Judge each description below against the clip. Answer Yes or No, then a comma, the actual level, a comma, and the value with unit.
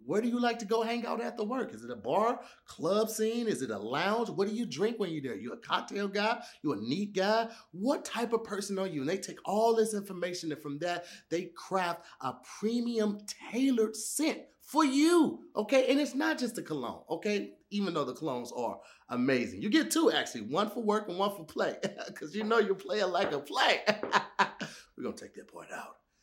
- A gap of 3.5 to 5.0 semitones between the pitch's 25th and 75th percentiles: Yes, average, 4.5 semitones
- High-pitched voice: Yes, high, 210 Hz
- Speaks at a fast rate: Yes, fast, 225 wpm